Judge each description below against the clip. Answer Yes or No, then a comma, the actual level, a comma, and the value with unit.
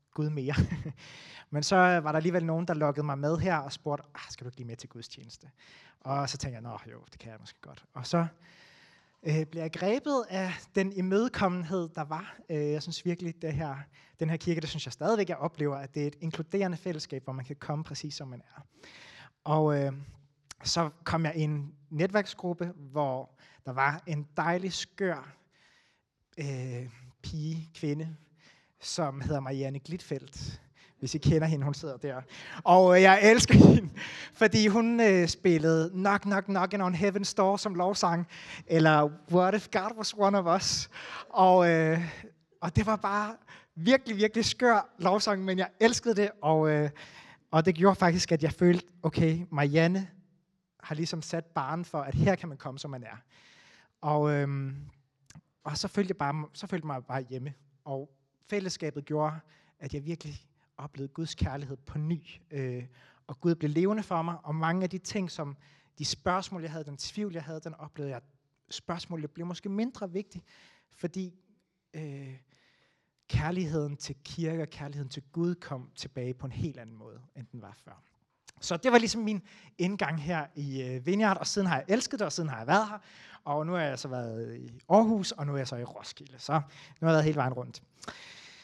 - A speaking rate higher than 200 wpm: No, average, 190 wpm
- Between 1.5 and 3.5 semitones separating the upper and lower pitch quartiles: No, average, 4.3 semitones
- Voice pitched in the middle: Yes, medium, 160 Hz